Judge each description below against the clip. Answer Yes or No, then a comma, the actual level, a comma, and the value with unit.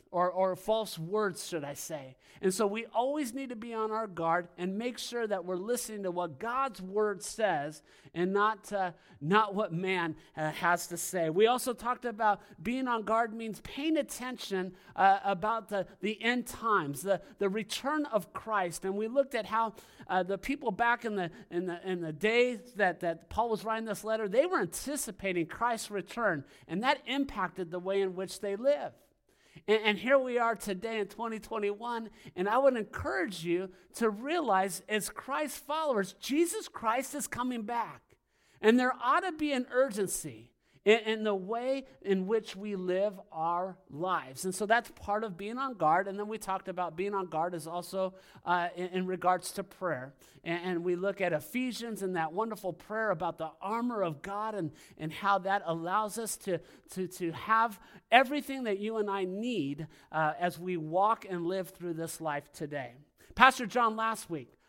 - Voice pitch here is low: No, high, 205 Hz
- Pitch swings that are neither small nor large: Yes, average, 4.3 semitones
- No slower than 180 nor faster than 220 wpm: Yes, average, 185 wpm